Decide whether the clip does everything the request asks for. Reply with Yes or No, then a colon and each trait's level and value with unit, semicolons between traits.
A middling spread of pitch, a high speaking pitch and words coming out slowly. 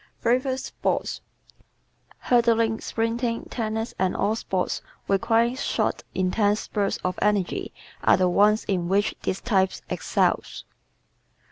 Yes: average, 3.2 semitones; high, 215 Hz; slow, 120 wpm